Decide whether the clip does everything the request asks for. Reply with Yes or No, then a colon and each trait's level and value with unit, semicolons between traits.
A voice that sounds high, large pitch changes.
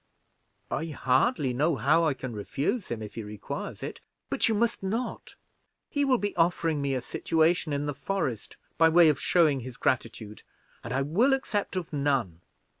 No: medium, 150 Hz; wide, 5.7 semitones